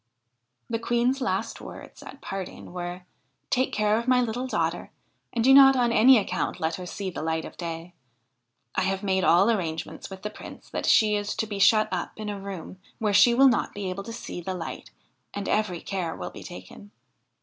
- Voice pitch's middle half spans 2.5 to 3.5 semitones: No, average, 4.3 semitones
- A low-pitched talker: No, high, 200 Hz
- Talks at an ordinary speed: No, fast, 210 wpm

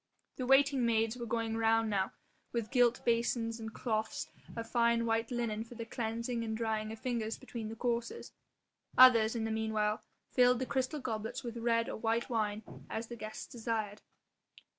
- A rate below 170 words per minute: No, average, 180 wpm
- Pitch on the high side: Yes, high, 230 Hz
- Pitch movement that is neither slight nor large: No, narrow, 1.4 semitones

